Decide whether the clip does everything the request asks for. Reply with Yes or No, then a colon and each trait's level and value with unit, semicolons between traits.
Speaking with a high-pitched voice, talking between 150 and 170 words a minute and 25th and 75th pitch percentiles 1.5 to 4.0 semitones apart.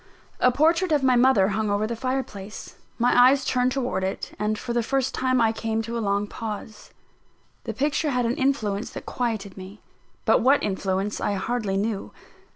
No: high, 230 Hz; average, 185 wpm; average, 3.7 semitones